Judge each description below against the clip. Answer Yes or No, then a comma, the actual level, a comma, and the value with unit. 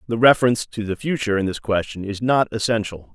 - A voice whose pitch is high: No, low, 110 Hz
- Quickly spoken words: Yes, fast, 210 wpm